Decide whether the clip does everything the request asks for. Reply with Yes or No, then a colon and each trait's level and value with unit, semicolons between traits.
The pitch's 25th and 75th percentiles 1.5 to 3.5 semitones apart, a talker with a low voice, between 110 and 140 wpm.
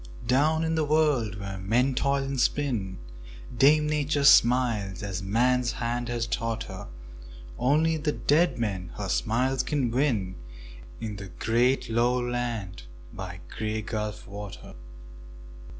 No: average, 4.8 semitones; low, 120 Hz; slow, 135 wpm